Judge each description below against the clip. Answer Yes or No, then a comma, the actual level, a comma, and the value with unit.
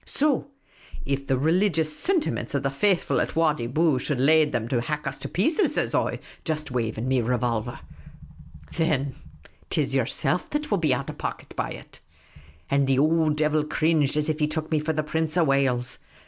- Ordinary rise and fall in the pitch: Yes, average, 3.4 semitones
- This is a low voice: No, medium, 150 Hz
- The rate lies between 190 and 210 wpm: Yes, average, 200 wpm